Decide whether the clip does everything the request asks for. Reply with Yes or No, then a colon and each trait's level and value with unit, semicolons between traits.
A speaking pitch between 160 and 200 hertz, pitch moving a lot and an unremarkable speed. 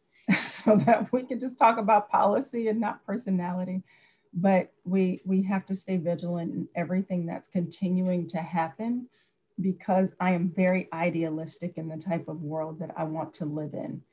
No: medium, 185 Hz; average, 2.7 semitones; average, 170 wpm